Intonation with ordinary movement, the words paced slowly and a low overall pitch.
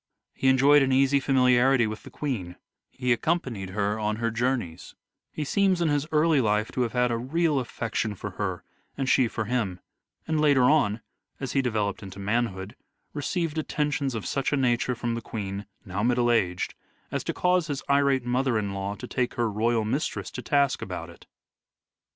No: average, 4.6 semitones; average, 185 wpm; low, 125 Hz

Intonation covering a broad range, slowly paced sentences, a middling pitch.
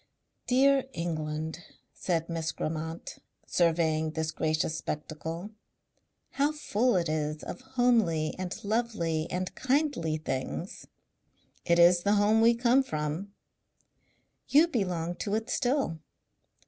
Yes: wide, 6.4 semitones; slow, 115 wpm; medium, 175 Hz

